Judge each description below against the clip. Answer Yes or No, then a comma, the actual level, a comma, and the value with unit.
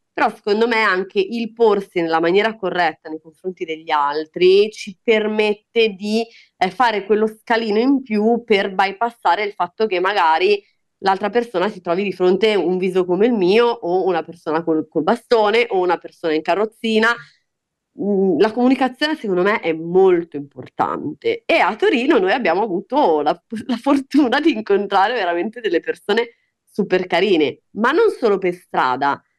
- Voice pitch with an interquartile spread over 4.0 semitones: Yes, average, 4.5 semitones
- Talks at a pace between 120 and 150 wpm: No, average, 160 wpm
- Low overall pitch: No, high, 205 Hz